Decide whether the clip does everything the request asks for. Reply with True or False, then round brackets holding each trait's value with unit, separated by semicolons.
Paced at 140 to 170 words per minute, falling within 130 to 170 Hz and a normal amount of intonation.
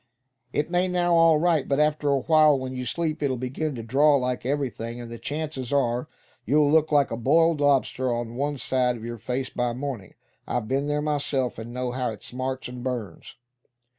False (200 wpm; 135 Hz; 3.4 semitones)